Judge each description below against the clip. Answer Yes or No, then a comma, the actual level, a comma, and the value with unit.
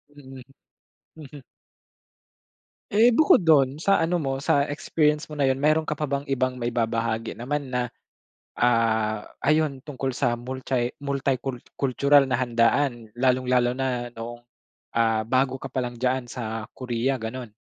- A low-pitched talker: Yes, low, 130 Hz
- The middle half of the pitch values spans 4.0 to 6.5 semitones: No, average, 2.8 semitones